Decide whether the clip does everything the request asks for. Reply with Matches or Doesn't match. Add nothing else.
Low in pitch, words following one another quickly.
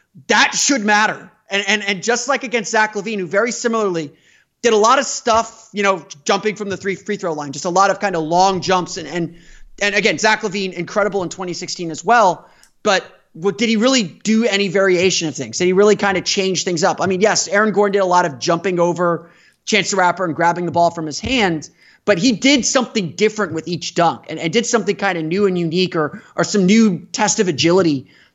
Doesn't match